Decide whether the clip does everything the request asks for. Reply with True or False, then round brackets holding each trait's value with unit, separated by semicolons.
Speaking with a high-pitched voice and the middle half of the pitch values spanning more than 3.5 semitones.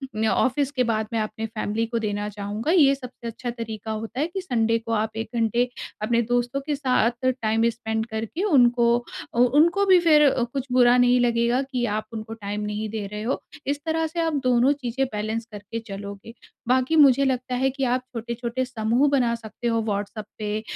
False (235 Hz; 3.0 semitones)